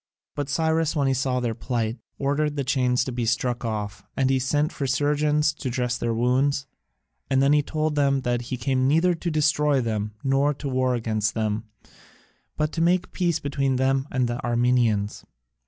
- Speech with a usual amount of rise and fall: Yes, average, 3.3 semitones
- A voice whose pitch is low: Yes, low, 130 Hz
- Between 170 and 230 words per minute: Yes, average, 185 wpm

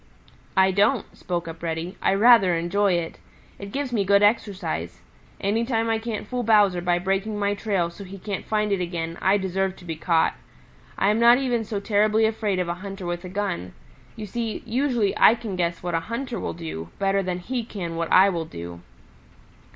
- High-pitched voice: Yes, high, 195 Hz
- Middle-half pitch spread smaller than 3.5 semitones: No, average, 3.9 semitones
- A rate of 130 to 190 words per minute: No, fast, 205 wpm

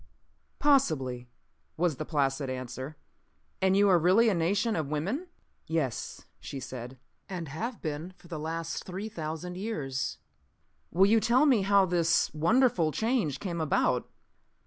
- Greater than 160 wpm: No, average, 145 wpm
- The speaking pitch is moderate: Yes, medium, 170 Hz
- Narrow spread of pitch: No, wide, 5.4 semitones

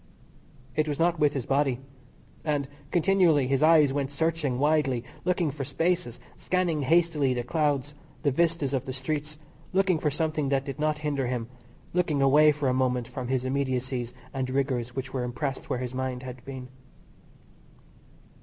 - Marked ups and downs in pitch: No, average, 3.0 semitones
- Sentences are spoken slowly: No, average, 165 wpm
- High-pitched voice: No, medium, 140 Hz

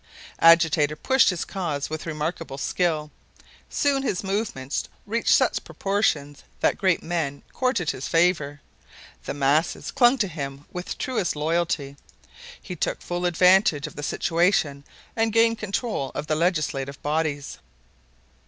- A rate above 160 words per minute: No, slow, 135 wpm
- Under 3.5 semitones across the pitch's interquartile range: No, average, 4.7 semitones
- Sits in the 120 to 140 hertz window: No, medium, 165 Hz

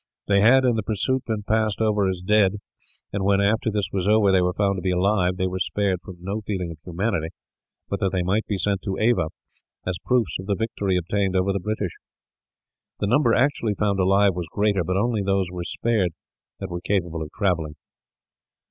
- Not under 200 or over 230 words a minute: Yes, fast, 205 wpm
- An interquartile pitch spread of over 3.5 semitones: No, narrow, 2.5 semitones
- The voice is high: No, low, 100 Hz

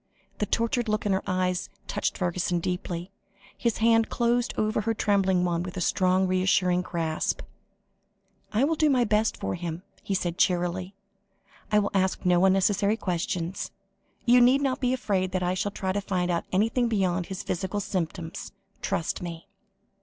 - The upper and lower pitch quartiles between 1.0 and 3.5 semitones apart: Yes, average, 3.2 semitones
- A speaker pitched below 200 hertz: Yes, high, 190 Hz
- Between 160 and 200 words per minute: Yes, average, 170 wpm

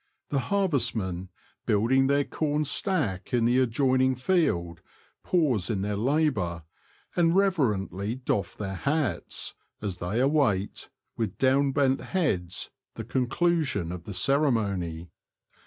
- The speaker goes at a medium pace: No, slow, 125 wpm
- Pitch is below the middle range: Yes, low, 125 Hz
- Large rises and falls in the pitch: Yes, wide, 6.8 semitones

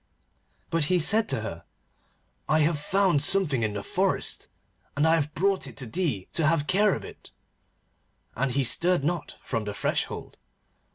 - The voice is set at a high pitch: No, medium, 155 Hz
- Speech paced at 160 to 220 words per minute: Yes, average, 170 wpm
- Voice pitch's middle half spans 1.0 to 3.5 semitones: No, average, 5.2 semitones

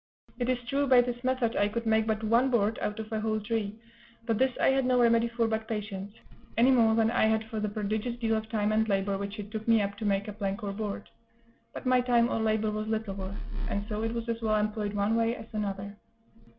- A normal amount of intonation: No, narrow, 1.9 semitones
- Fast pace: Yes, fast, 250 wpm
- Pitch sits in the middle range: No, high, 220 Hz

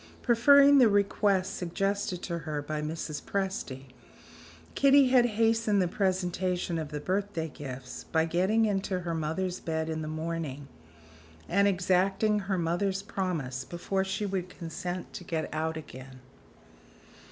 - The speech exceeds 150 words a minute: No, average, 140 wpm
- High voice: No, medium, 180 Hz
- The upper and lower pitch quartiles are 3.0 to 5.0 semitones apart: Yes, average, 3.8 semitones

